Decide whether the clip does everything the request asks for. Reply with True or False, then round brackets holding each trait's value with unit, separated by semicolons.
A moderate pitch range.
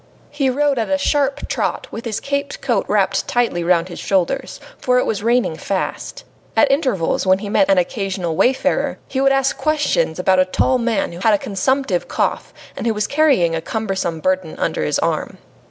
False (6.5 semitones)